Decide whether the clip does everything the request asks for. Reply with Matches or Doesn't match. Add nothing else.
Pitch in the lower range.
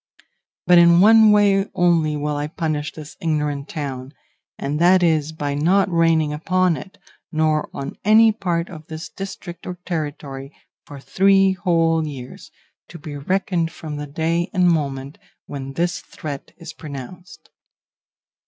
Doesn't match